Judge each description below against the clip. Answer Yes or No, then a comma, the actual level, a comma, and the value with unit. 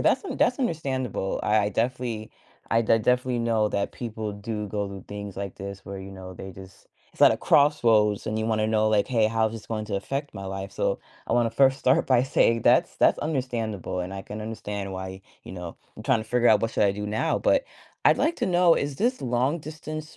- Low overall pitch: Yes, low, 110 Hz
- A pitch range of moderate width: Yes, average, 4.1 semitones